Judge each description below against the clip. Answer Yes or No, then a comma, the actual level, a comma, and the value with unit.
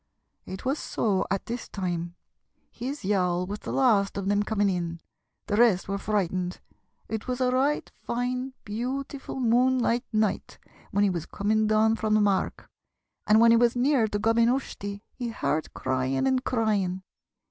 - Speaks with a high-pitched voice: Yes, high, 215 Hz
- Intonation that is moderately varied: Yes, average, 4.1 semitones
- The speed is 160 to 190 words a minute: Yes, average, 170 wpm